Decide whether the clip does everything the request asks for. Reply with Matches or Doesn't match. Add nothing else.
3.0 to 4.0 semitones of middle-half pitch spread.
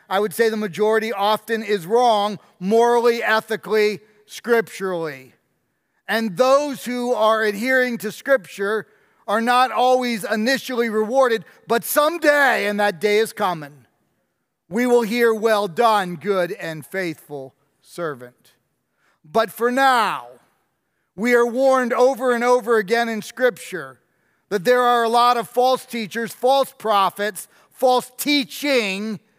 Matches